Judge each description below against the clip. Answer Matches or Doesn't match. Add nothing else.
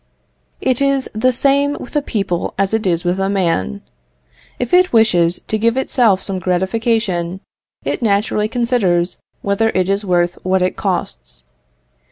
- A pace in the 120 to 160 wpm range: Matches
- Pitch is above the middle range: Matches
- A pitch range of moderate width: Matches